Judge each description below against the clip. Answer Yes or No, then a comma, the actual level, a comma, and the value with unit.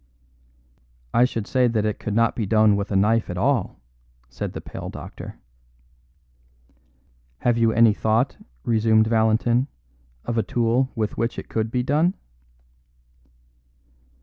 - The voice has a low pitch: Yes, low, 115 Hz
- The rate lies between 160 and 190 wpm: No, average, 140 wpm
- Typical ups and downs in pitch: No, narrow, 1.8 semitones